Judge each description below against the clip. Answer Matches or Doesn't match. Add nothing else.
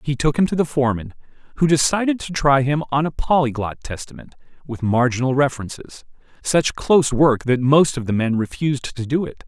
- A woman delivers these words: Doesn't match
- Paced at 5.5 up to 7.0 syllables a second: Matches